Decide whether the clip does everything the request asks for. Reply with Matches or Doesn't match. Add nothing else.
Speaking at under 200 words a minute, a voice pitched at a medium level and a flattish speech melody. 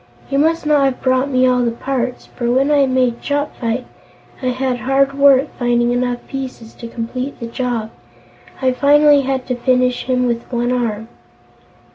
Doesn't match